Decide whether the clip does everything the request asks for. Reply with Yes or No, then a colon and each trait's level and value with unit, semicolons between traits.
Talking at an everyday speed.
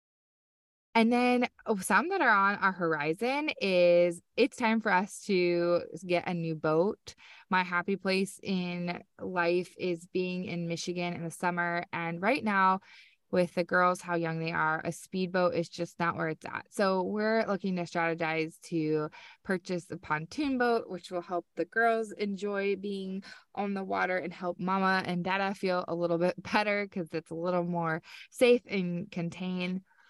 Yes: average, 170 wpm